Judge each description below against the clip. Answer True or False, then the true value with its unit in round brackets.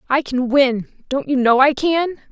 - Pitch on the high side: True (275 Hz)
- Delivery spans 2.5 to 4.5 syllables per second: True (4.1 syllables/s)